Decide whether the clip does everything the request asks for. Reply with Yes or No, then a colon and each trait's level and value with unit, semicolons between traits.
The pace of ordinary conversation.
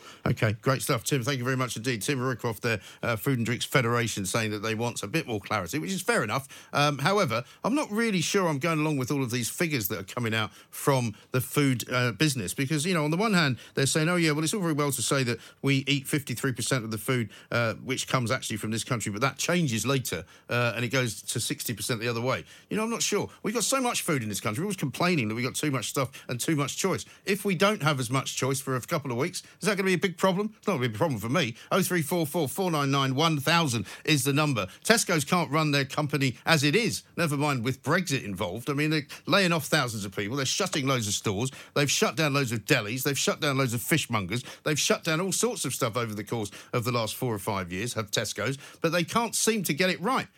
No: fast, 265 wpm